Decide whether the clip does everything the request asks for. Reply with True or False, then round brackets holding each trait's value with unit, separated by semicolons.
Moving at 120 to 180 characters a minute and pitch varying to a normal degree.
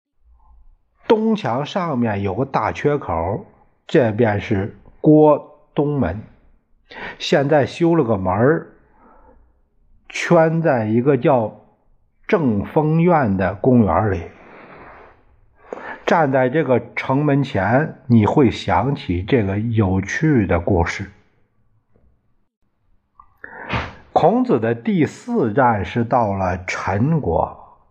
False (135 characters per minute; 7.2 semitones)